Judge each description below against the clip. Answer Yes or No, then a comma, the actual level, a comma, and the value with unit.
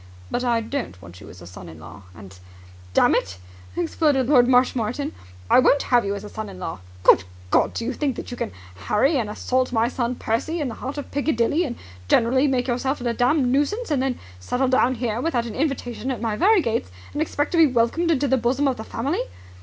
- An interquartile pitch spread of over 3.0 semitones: Yes, average, 3.8 semitones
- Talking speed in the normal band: No, fast, 225 wpm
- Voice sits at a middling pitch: No, very high, 250 Hz